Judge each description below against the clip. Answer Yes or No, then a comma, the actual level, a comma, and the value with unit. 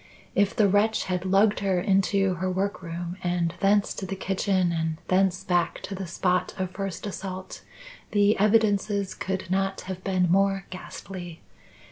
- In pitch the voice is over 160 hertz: Yes, high, 190 Hz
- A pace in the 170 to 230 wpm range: No, average, 155 wpm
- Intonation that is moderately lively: No, narrow, 1.6 semitones